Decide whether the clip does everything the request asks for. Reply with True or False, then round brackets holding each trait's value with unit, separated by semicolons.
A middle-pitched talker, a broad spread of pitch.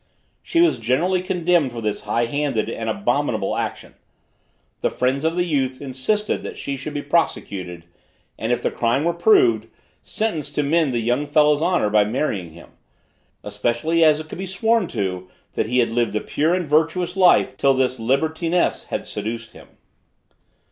True (145 Hz; 6.3 semitones)